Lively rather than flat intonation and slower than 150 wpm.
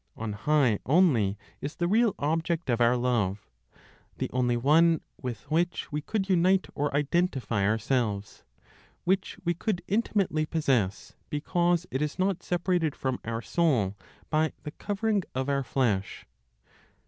Yes: wide, 6.4 semitones; average, 140 wpm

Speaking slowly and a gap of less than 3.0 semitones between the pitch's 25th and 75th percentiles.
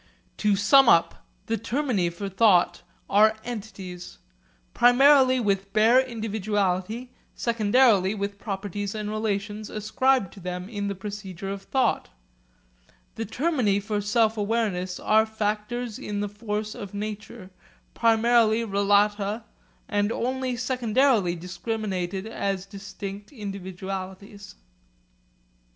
Yes: slow, 110 wpm; narrow, 2.5 semitones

